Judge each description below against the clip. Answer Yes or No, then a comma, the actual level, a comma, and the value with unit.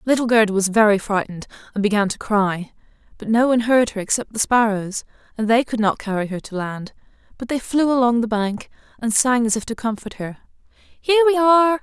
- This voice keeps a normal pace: No, fast, 210 wpm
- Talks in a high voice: Yes, high, 230 Hz